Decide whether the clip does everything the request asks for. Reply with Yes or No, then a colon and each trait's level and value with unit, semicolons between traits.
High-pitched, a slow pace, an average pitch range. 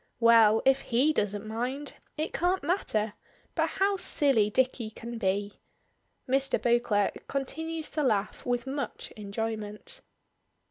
Yes: high, 240 Hz; slow, 125 wpm; average, 5.0 semitones